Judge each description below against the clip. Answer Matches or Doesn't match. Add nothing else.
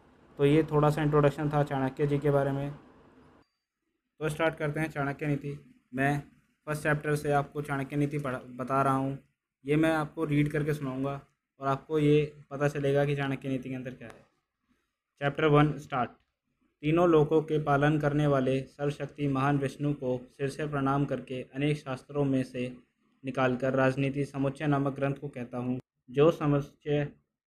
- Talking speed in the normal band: Matches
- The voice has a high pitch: Doesn't match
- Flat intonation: Matches